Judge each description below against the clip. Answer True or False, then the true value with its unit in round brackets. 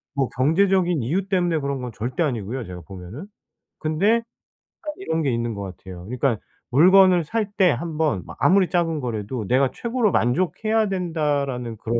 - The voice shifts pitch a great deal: True (7.5 semitones)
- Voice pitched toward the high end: False (150 Hz)